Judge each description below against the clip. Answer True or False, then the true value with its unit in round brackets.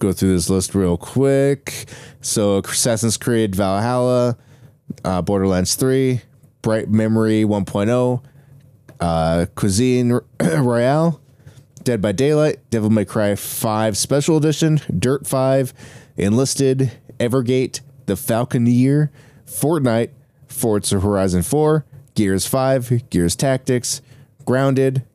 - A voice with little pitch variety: False (3.9 semitones)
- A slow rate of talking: True (105 wpm)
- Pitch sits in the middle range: False (125 Hz)